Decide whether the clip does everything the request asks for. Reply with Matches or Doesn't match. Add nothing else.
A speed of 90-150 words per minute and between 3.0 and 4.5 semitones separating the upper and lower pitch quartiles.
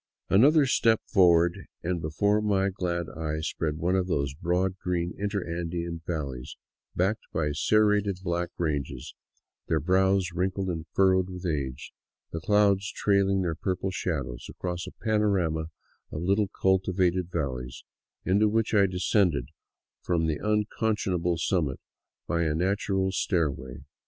Matches